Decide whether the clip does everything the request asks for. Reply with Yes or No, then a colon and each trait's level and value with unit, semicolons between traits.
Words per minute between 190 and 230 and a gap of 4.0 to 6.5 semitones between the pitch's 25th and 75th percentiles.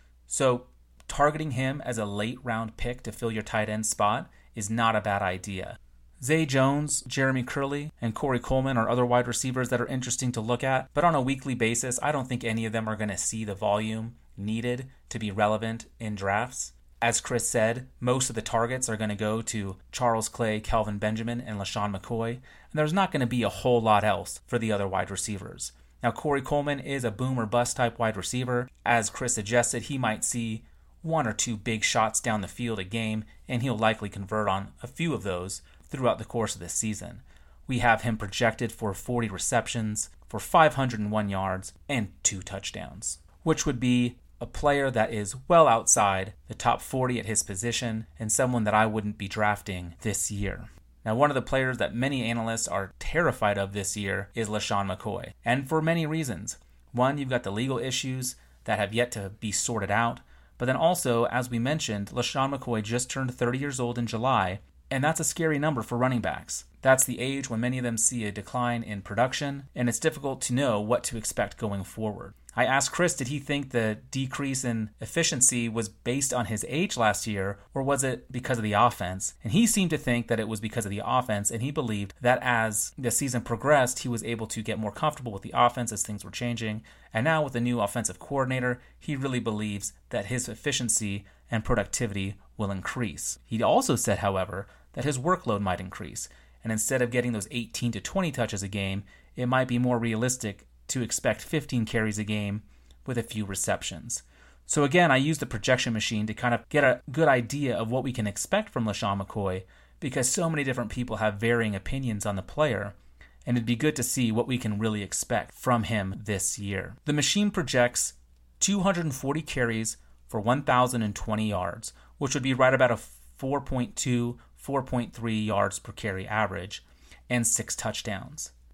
No: average, 200 wpm; average, 3.5 semitones